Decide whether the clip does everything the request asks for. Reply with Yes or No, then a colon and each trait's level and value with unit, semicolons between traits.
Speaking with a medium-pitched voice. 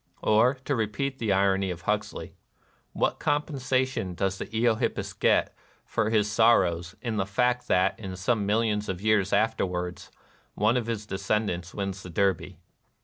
No: low, 105 Hz